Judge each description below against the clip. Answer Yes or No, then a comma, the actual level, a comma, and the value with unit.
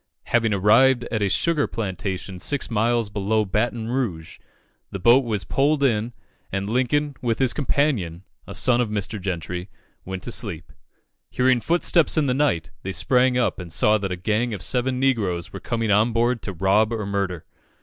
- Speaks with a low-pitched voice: Yes, low, 110 Hz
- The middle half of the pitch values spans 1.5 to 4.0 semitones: No, average, 4.5 semitones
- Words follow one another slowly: No, average, 180 wpm